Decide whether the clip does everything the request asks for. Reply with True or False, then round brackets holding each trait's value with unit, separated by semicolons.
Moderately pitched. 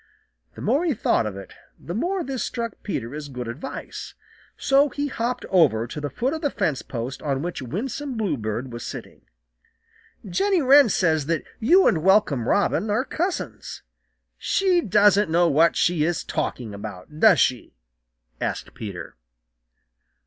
True (175 Hz)